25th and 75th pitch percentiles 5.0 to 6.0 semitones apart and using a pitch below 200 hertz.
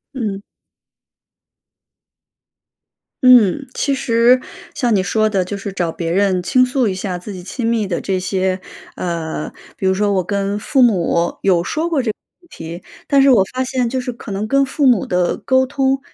No: wide, 5.5 semitones; high, 210 Hz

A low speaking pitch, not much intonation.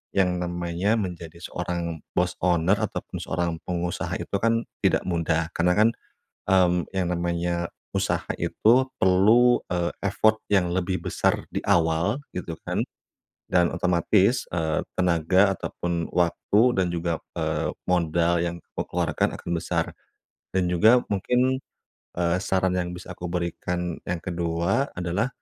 Yes: very low, 90 Hz; narrow, 1.8 semitones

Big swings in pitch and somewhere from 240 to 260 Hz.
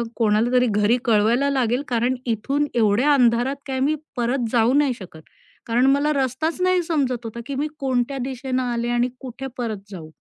No: average, 2.8 semitones; very high, 250 Hz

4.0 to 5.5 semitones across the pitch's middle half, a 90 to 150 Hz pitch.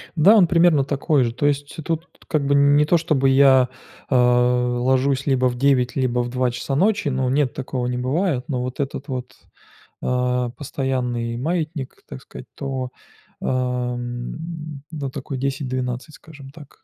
No: average, 2.7 semitones; low, 135 Hz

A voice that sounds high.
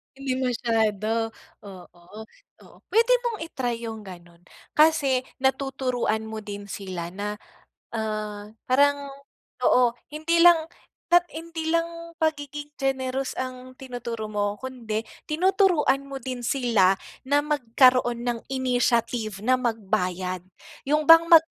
Yes: very high, 255 Hz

